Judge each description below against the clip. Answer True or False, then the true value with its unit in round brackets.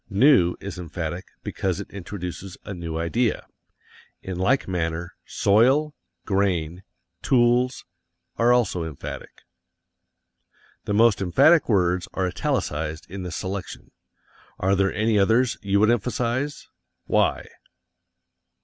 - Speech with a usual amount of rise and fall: True (4.9 semitones)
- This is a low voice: True (100 Hz)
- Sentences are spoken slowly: True (115 wpm)